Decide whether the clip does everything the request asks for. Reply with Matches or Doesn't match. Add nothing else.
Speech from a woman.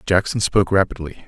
Doesn't match